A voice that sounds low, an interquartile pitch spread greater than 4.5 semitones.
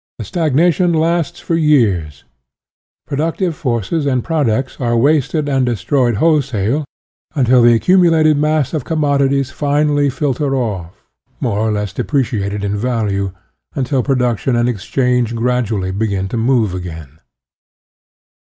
Yes: low, 130 Hz; average, 5.2 semitones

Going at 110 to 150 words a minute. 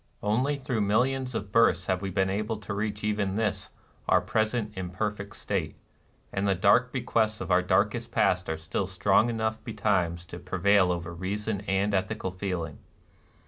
No: average, 165 wpm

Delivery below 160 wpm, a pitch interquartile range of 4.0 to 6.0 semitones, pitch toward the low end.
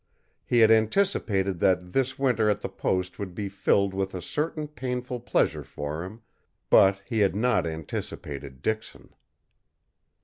Yes: average, 145 wpm; average, 5.0 semitones; low, 100 Hz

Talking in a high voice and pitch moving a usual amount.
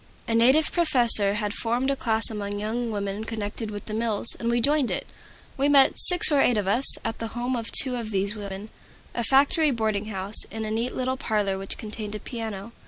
Yes: high, 225 Hz; average, 3.0 semitones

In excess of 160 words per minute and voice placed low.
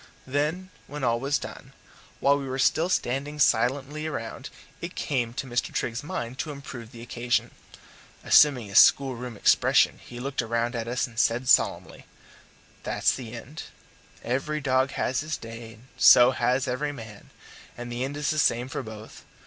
Yes: average, 170 wpm; low, 130 Hz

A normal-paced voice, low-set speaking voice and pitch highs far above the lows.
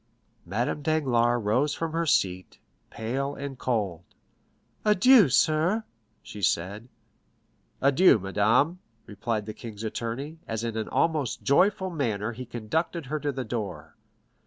No: slow, 130 wpm; low, 125 Hz; wide, 6.3 semitones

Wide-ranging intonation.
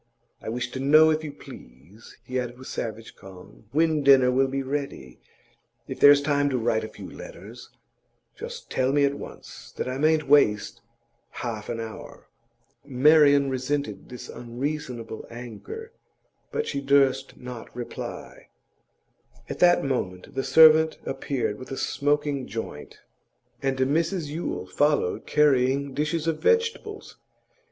No: average, 3.6 semitones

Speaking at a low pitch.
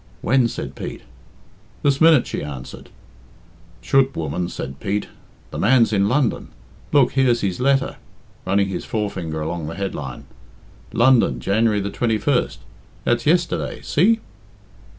Yes: low, 110 Hz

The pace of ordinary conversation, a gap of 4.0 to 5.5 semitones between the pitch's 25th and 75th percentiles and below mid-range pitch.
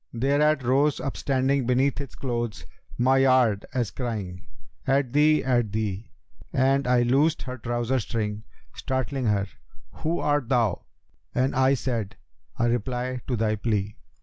No: average, 150 wpm; average, 2.8 semitones; low, 125 Hz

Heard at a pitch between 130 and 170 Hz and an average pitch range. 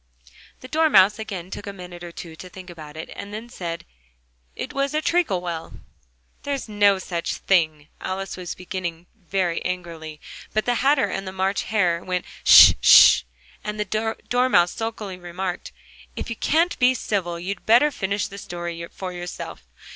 No: high, 190 Hz; average, 3.9 semitones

